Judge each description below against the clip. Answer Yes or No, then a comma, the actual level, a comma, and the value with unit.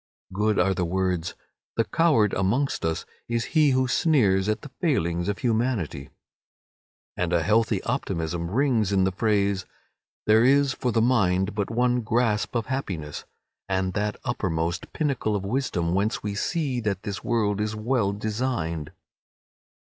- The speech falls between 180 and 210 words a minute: No, average, 150 wpm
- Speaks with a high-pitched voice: No, low, 105 Hz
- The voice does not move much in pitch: No, average, 4.6 semitones